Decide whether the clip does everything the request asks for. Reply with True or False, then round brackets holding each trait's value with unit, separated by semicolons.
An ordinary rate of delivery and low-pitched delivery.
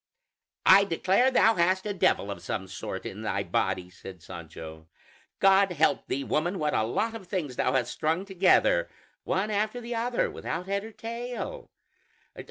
False (170 wpm; 185 Hz)